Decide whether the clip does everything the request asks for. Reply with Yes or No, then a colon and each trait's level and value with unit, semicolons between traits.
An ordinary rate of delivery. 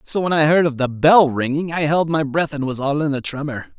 No: fast, 285 wpm